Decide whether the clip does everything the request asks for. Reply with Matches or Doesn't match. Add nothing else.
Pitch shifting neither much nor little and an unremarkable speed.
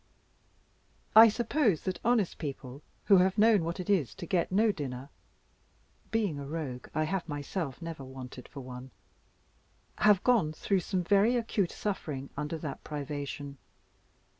Doesn't match